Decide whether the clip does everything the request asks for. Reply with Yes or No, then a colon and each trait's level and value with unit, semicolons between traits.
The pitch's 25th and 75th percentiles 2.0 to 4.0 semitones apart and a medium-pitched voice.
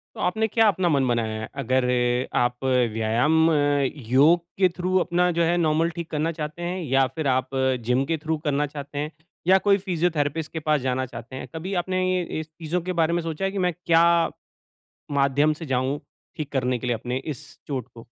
No: average, 4.8 semitones; medium, 150 Hz